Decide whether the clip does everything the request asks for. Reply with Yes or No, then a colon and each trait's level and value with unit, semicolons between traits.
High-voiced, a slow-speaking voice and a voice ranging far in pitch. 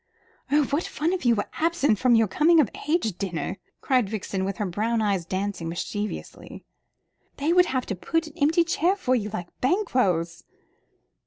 No: high, 235 Hz; average, 175 wpm; wide, 7.9 semitones